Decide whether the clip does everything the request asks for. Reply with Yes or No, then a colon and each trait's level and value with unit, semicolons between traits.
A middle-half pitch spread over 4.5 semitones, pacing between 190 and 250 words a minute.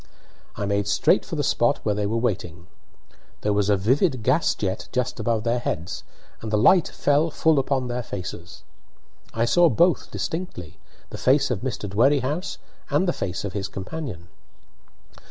No: wide, 5.6 semitones; average, 170 wpm